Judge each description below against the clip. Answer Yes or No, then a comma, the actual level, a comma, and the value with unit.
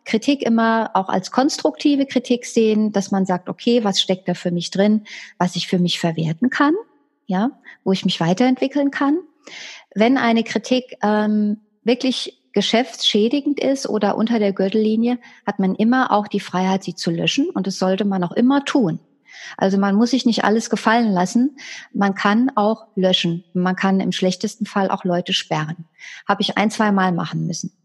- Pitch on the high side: Yes, high, 210 Hz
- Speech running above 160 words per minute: Yes, average, 175 wpm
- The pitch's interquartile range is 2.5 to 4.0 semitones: No, average, 4.4 semitones